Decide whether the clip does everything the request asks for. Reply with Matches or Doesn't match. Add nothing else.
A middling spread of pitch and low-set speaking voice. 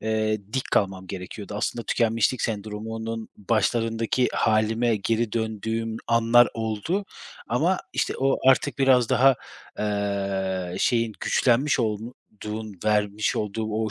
Doesn't match